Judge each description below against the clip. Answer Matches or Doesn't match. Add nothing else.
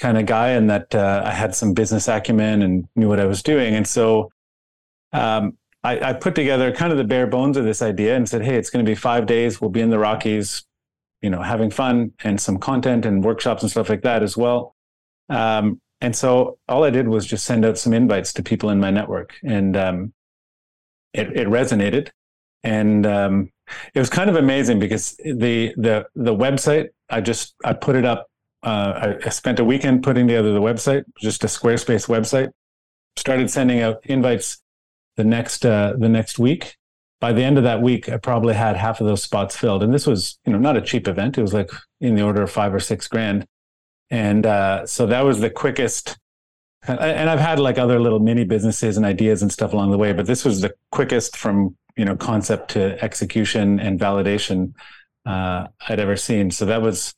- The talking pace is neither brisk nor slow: Doesn't match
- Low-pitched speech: Matches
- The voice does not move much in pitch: Doesn't match